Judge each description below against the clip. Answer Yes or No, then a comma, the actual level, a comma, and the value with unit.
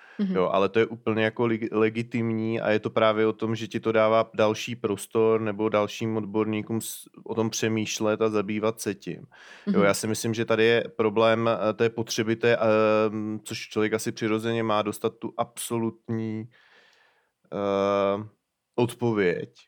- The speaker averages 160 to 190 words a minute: No, average, 150 wpm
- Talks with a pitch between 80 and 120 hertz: Yes, low, 110 Hz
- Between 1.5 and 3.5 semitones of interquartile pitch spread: No, narrow, 1.0 semitones